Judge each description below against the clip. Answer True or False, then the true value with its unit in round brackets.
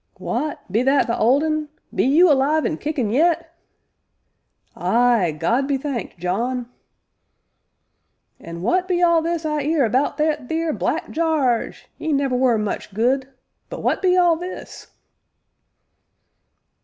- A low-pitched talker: False (280 Hz)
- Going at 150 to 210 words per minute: False (140 wpm)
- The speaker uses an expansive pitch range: False (4.7 semitones)